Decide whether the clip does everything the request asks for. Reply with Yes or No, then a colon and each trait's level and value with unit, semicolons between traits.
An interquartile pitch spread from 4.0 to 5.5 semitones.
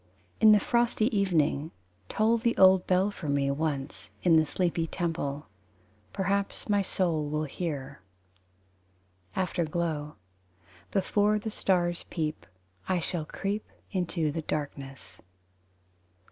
Yes: average, 4.5 semitones